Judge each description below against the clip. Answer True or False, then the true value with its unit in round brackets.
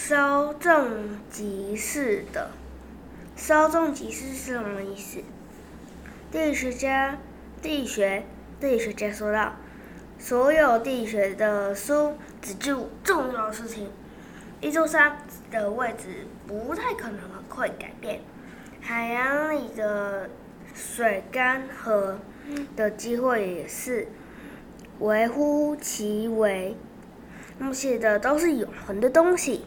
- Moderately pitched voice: False (240 Hz)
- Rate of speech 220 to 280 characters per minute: False (165 characters per minute)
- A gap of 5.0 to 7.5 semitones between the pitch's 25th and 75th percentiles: True (5.3 semitones)